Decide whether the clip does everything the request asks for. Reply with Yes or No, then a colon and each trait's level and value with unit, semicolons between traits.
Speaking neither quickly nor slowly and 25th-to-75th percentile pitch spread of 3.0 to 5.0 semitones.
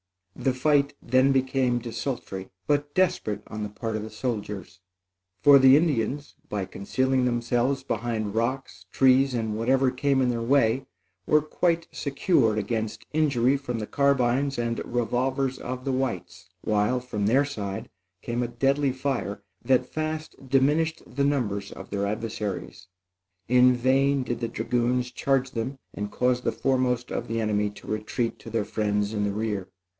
Yes: average, 160 wpm; average, 3.6 semitones